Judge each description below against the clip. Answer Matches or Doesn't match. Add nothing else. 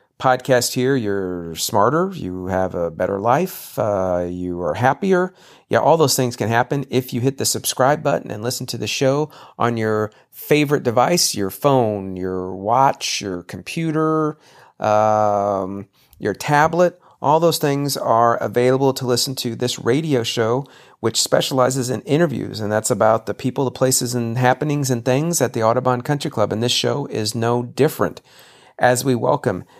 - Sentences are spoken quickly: Doesn't match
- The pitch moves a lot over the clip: Doesn't match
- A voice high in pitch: Doesn't match